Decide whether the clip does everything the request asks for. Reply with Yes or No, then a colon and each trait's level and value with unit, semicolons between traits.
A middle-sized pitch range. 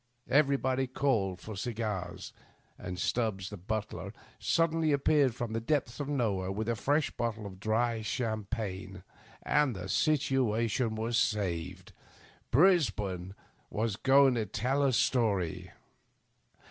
Yes: average, 4.8 semitones